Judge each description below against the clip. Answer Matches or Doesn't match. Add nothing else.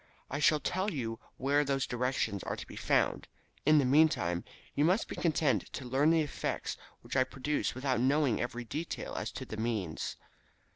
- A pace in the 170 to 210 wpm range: Matches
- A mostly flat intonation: Doesn't match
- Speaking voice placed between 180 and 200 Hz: Doesn't match